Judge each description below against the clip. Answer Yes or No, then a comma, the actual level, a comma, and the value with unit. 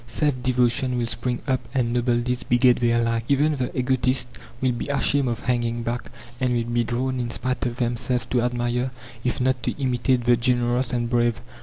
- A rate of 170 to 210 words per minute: Yes, average, 195 wpm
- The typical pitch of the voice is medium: No, low, 125 Hz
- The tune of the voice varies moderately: No, narrow, 1.2 semitones